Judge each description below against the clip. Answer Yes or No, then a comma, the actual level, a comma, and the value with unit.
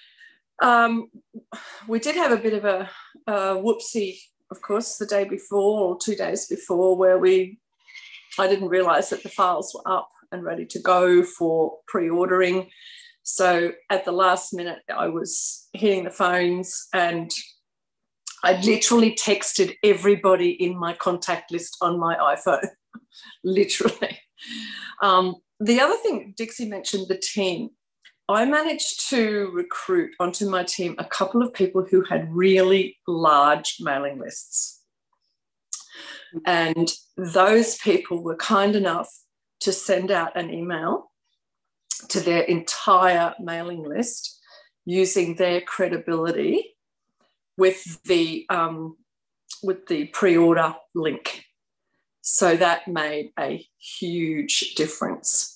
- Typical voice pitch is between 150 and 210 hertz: Yes, high, 190 Hz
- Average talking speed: No, slow, 125 wpm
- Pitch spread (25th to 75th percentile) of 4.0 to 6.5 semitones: Yes, average, 4.4 semitones